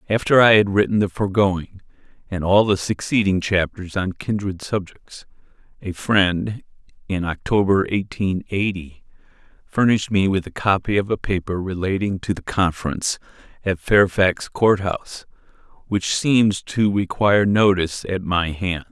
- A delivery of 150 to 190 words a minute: No, average, 140 wpm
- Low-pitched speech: Yes, very low, 95 Hz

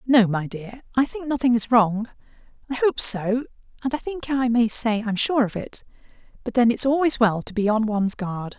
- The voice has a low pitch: No, high, 235 Hz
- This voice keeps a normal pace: No, fast, 215 wpm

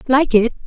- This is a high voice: Yes, very high, 250 Hz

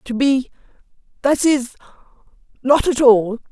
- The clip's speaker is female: Yes, female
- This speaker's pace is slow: Yes, slow, 100 wpm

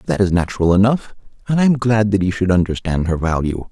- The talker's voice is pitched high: No, low, 100 Hz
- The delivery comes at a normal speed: No, fast, 225 wpm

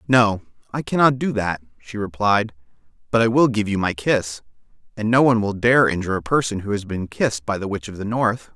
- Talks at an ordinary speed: No, fast, 225 wpm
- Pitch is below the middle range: Yes, low, 110 Hz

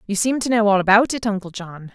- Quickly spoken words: Yes, fast, 275 wpm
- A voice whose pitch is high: Yes, high, 210 Hz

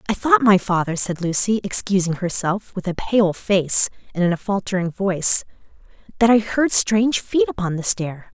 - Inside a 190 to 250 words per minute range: No, average, 180 wpm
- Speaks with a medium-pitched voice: No, high, 195 Hz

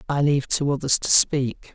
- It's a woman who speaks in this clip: No, male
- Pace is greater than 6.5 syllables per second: No, 5.1 syllables/s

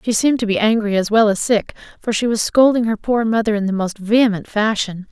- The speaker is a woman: Yes, female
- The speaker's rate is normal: No, fast, 245 wpm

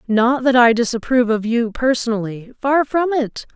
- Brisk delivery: No, average, 150 wpm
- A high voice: Yes, high, 240 Hz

